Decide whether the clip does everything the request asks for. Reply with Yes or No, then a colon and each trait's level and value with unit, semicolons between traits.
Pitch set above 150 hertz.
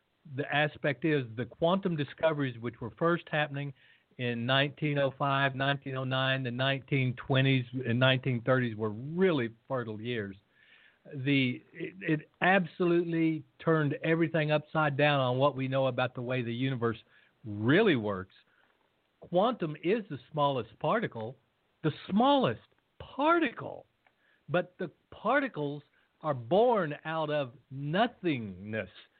No: medium, 140 Hz